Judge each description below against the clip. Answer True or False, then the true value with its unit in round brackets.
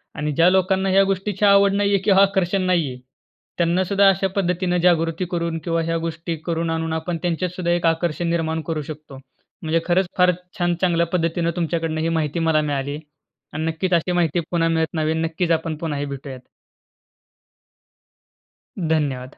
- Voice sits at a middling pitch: True (170 Hz)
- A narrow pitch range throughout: True (2.1 semitones)